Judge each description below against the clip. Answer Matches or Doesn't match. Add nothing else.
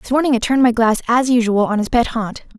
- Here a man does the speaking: Doesn't match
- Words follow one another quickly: Matches